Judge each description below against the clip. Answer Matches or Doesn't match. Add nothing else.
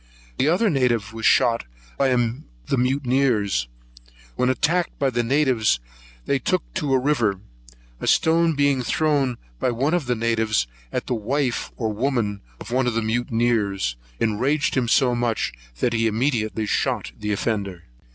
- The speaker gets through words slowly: Doesn't match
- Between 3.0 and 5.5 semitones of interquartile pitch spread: Matches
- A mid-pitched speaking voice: Doesn't match